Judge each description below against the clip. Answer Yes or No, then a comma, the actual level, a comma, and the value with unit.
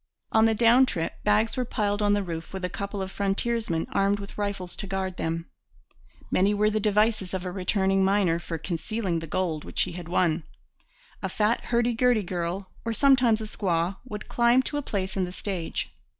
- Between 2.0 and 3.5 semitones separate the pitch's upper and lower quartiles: Yes, average, 3.2 semitones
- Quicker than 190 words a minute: Yes, average, 200 wpm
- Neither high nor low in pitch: No, high, 200 Hz